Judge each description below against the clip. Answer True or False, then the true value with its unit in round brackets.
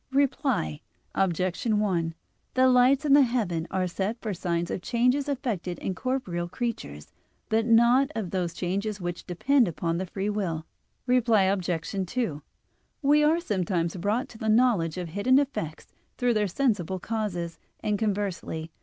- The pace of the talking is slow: False (155 wpm)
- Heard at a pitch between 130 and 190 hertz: False (200 Hz)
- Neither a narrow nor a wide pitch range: False (5.8 semitones)